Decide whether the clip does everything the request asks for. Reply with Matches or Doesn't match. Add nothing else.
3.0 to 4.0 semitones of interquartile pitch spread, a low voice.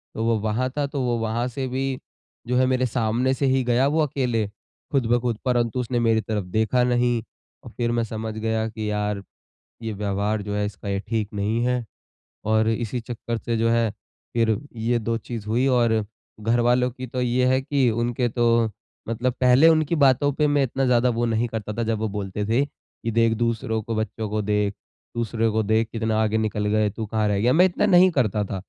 Doesn't match